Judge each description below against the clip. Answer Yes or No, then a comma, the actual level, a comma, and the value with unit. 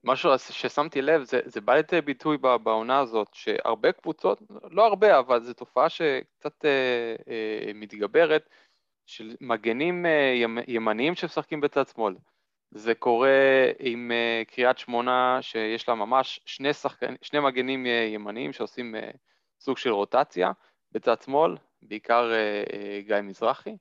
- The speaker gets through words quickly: No, average, 135 wpm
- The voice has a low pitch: Yes, low, 125 Hz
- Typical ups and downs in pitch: Yes, average, 3.9 semitones